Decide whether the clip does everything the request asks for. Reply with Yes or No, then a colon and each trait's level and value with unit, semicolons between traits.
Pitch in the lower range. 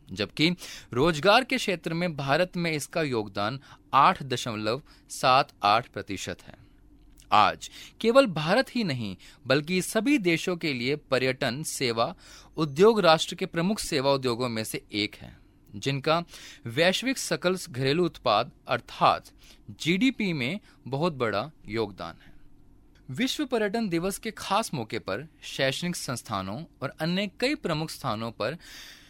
No: medium, 155 Hz